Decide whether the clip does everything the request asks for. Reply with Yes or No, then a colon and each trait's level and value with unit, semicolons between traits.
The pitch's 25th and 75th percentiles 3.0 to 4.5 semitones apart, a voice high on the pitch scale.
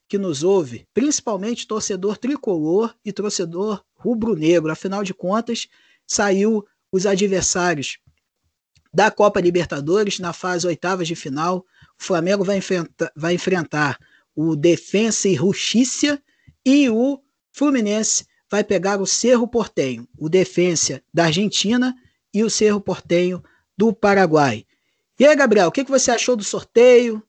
Yes: average, 4.1 semitones; high, 200 Hz